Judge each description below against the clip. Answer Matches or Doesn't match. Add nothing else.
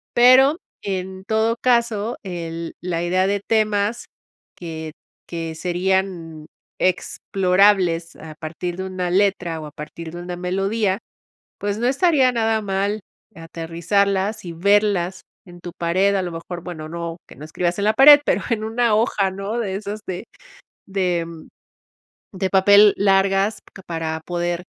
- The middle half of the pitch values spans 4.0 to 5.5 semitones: Doesn't match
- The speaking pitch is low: Doesn't match